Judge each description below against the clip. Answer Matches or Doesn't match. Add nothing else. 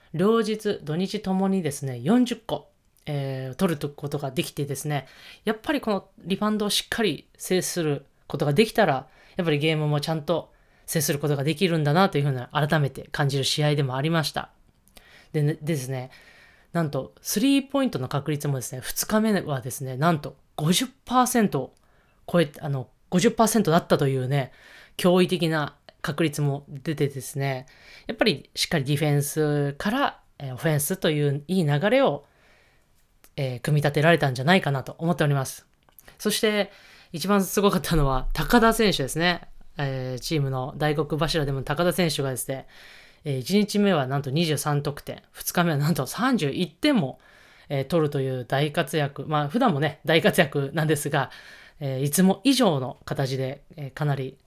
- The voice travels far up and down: Doesn't match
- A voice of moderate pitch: Matches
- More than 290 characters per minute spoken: Matches